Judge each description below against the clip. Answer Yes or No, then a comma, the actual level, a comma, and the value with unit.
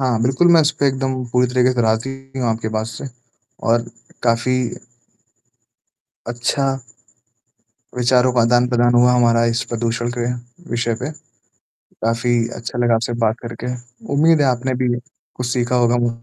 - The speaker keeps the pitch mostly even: Yes, narrow, 1.5 semitones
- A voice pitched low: Yes, low, 120 Hz